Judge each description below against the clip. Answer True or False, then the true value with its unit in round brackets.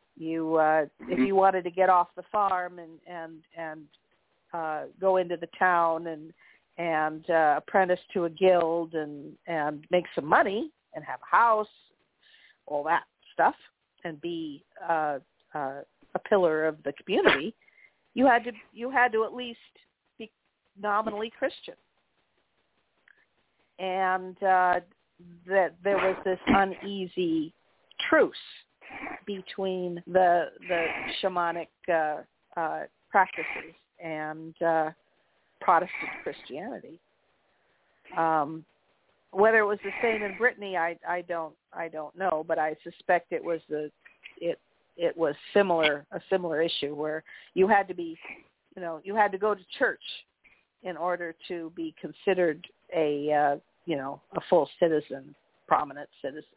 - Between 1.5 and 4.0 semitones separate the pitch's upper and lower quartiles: True (3.3 semitones)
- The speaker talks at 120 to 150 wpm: True (140 wpm)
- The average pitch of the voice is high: False (175 Hz)